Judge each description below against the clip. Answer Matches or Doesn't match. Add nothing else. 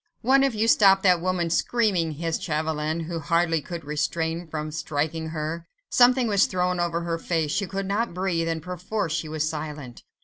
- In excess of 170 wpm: Matches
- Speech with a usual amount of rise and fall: Matches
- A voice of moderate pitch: Matches